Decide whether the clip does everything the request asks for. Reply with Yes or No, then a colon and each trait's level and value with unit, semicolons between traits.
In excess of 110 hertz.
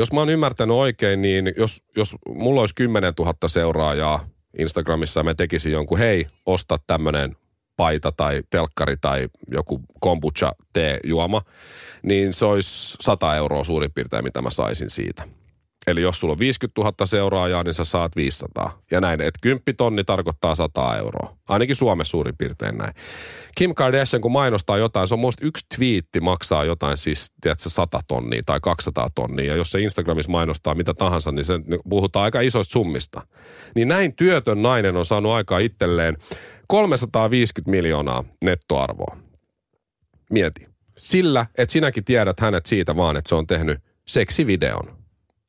No: very low, 95 Hz